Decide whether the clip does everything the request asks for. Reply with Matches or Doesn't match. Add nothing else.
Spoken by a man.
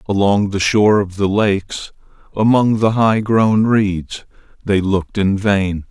Matches